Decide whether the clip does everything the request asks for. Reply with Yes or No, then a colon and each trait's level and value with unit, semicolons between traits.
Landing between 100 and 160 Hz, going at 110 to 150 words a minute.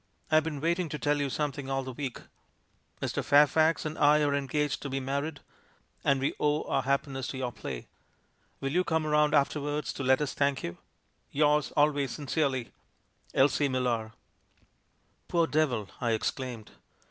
No: medium, 140 Hz; average, 180 wpm